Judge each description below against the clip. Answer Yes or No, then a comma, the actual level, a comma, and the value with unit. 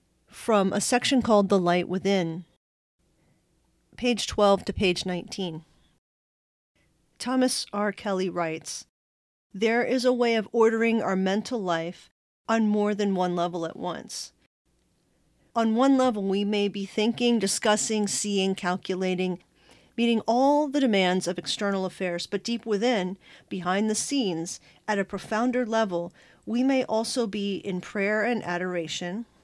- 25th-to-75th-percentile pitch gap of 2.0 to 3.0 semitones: No, average, 4.0 semitones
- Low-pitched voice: No, high, 205 Hz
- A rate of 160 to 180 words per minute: No, slow, 135 wpm